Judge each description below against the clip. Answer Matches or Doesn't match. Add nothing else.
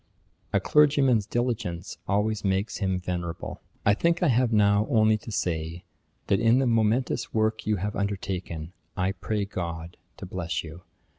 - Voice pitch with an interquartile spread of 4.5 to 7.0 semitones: Doesn't match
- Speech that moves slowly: Doesn't match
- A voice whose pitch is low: Matches